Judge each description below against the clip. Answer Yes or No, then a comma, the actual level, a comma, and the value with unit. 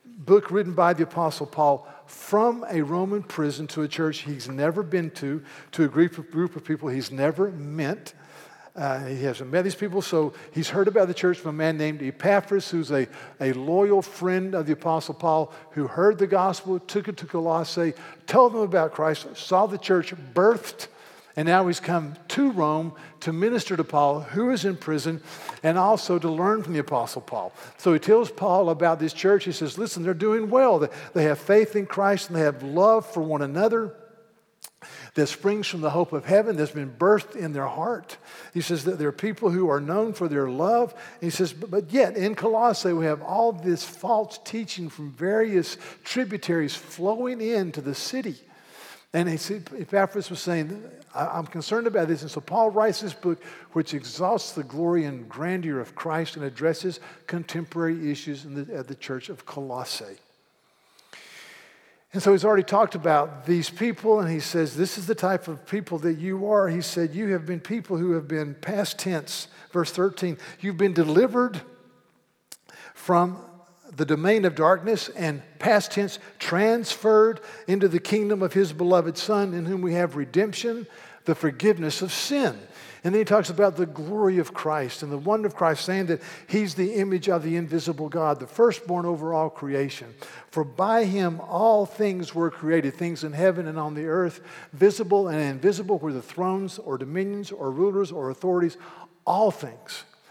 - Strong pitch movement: No, average, 4.3 semitones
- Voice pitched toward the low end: No, medium, 175 Hz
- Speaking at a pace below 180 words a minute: No, average, 185 wpm